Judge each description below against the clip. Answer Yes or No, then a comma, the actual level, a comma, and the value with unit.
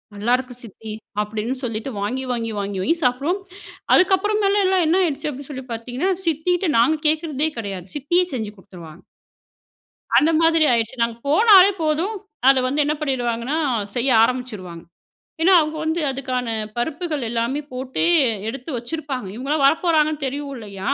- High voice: Yes, very high, 270 Hz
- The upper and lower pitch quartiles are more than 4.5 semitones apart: Yes, average, 5.3 semitones